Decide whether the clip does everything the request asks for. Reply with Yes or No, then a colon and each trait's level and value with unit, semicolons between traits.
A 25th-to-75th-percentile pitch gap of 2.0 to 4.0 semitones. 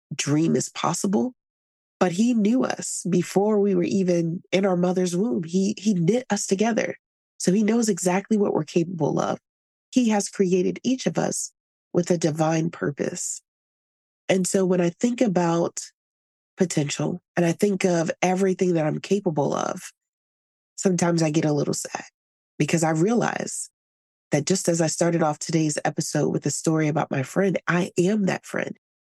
Yes: average, 3.3 semitones